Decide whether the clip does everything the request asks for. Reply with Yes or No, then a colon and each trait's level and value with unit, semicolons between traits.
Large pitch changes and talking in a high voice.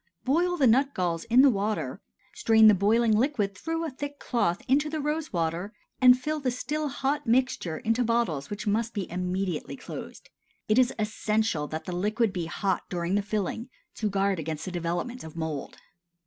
Yes: wide, 6.0 semitones; high, 215 Hz